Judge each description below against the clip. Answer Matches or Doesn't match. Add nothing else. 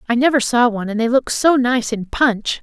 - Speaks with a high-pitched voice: Matches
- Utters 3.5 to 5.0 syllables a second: Doesn't match